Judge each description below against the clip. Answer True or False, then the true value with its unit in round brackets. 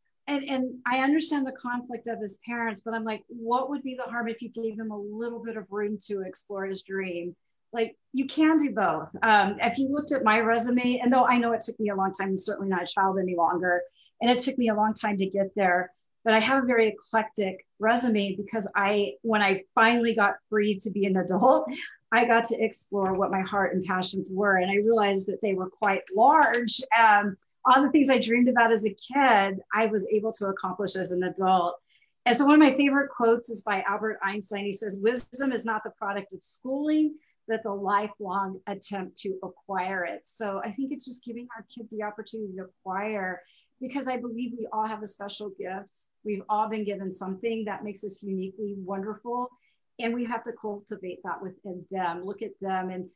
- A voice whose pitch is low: False (215 Hz)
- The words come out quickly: True (220 wpm)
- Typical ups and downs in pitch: True (3.3 semitones)